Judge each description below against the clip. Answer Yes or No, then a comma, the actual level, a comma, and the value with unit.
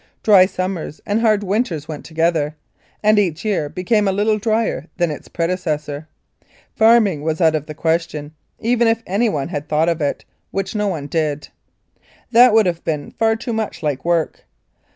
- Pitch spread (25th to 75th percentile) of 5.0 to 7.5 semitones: Yes, wide, 5.6 semitones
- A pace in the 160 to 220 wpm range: Yes, average, 175 wpm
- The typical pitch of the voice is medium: Yes, medium, 175 Hz